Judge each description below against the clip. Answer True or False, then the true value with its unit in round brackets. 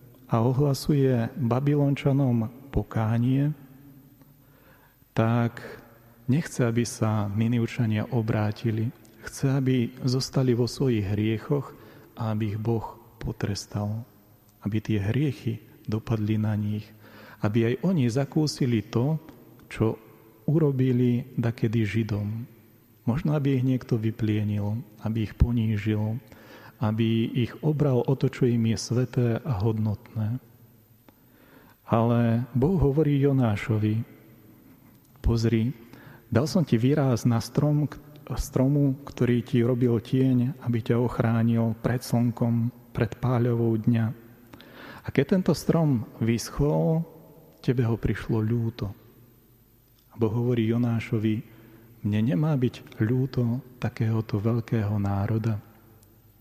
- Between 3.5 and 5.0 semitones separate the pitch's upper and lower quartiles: False (2.8 semitones)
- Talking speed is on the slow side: True (100 wpm)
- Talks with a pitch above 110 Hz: True (120 Hz)